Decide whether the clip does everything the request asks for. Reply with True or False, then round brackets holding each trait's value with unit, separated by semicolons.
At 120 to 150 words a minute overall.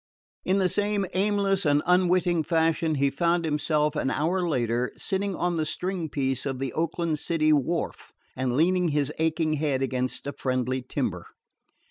False (160 wpm)